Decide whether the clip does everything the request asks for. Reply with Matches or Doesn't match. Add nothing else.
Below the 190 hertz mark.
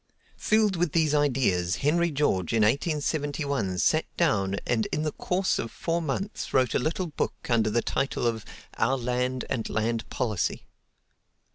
Matches